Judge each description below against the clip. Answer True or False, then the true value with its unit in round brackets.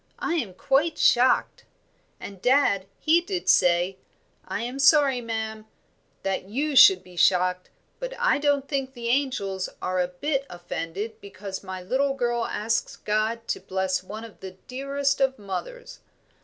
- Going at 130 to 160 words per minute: True (155 wpm)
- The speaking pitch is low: False (230 Hz)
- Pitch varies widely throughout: True (6.5 semitones)